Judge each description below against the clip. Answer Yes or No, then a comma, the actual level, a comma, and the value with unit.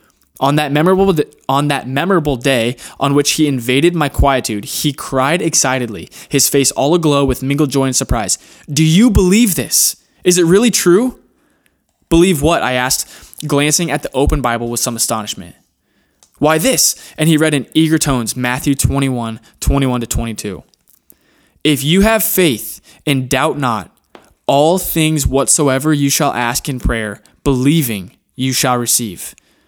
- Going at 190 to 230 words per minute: No, average, 160 wpm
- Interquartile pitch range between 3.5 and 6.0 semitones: Yes, average, 4.0 semitones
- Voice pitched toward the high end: No, medium, 140 Hz